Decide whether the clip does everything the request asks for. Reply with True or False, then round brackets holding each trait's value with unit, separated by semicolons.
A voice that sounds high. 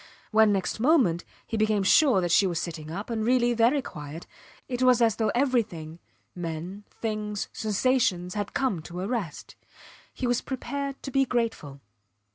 True (215 Hz)